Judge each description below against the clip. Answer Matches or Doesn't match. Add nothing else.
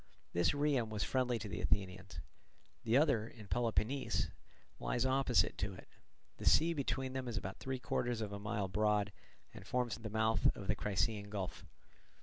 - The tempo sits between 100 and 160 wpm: Doesn't match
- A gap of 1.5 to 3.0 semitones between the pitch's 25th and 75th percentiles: Doesn't match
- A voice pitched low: Matches